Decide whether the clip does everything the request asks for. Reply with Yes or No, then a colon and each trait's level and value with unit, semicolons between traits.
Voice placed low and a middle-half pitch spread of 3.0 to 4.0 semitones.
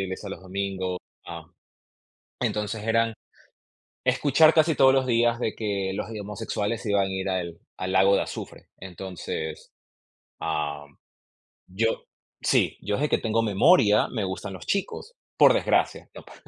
Yes: low, 100 Hz; average, 3.4 semitones